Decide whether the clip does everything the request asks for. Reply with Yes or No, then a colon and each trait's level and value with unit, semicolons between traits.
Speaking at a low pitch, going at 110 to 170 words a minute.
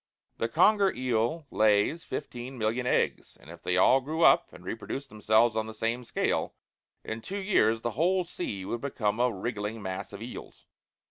No: low, 115 Hz; average, 180 wpm